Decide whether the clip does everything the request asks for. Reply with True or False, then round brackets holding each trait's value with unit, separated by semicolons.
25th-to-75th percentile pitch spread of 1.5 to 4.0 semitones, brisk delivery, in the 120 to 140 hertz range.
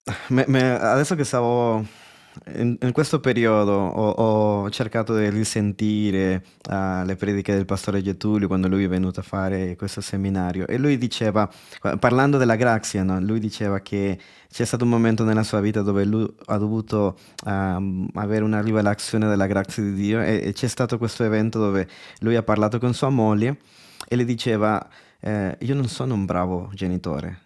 False (2.8 semitones; 175 wpm; 105 Hz)